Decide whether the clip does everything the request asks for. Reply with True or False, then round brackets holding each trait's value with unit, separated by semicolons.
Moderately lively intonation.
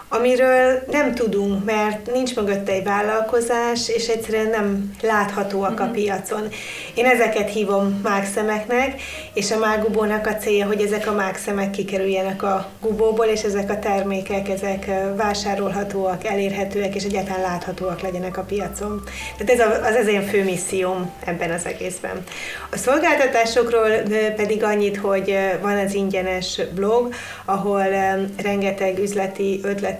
False (2.1 semitones)